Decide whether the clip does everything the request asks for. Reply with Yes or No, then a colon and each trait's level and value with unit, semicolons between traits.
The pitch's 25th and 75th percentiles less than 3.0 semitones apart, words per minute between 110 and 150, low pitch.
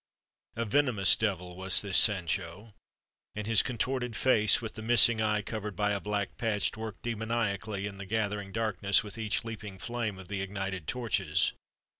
No: narrow, 2.4 semitones; average, 165 wpm; low, 105 Hz